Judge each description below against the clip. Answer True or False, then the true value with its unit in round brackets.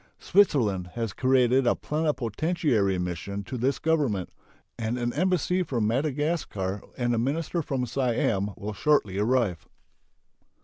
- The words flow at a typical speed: False (125 wpm)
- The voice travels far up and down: True (6.3 semitones)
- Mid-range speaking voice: False (120 Hz)